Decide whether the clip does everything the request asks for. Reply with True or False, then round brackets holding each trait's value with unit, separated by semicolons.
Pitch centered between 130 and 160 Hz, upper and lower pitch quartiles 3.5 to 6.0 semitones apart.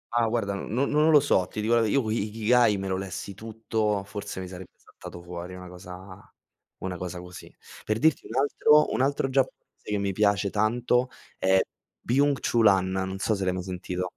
False (100 Hz; 4.1 semitones)